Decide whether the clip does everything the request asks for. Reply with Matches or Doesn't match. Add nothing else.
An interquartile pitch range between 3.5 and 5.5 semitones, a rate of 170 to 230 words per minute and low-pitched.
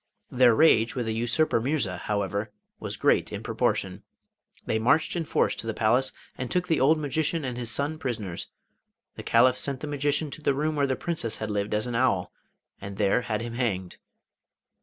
Matches